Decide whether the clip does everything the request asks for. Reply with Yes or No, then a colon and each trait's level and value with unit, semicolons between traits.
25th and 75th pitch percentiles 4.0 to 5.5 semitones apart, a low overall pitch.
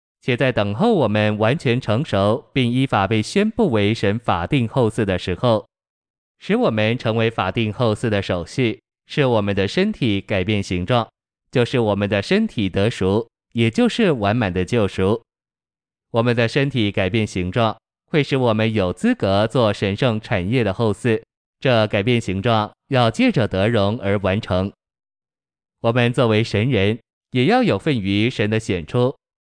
No: average, 3.5 semitones; low, 110 Hz